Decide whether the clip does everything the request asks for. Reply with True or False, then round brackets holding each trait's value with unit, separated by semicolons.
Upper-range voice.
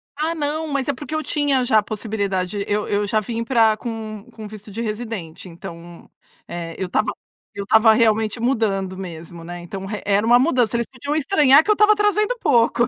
True (220 Hz)